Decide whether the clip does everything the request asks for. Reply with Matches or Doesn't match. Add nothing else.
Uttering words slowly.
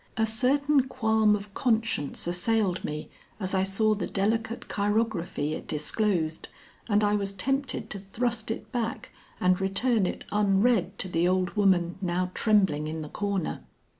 Doesn't match